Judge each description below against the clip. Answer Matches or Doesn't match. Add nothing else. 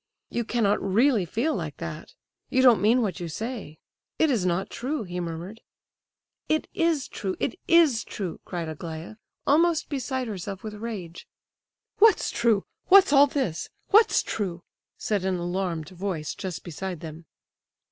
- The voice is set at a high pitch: Matches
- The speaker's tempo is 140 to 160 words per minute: Matches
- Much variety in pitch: Matches